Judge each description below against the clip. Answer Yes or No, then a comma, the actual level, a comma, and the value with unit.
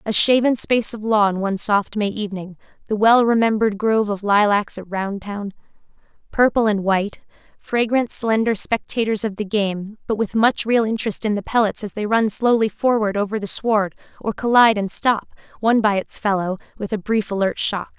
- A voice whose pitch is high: Yes, high, 210 Hz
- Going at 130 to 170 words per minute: No, average, 180 wpm